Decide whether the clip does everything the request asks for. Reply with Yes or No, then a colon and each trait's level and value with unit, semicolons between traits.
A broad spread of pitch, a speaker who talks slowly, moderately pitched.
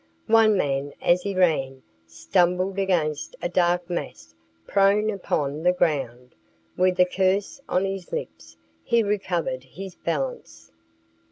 Yes: wide, 6.0 semitones; slow, 125 wpm; medium, 175 Hz